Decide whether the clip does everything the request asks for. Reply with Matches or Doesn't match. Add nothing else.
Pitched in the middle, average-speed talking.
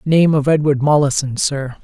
Matches